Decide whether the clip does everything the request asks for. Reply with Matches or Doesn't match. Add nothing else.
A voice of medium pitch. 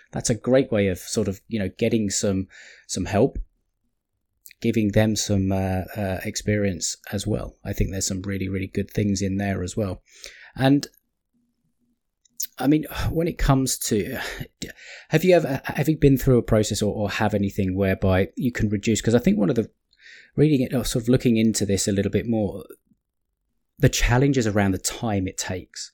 Doesn't match